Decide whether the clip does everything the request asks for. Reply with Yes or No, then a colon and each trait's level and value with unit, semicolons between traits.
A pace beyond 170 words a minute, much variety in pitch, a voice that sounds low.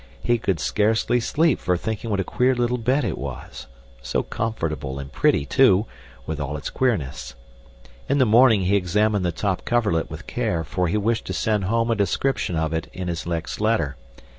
Yes: average, 190 wpm; wide, 5.9 semitones; low, 105 Hz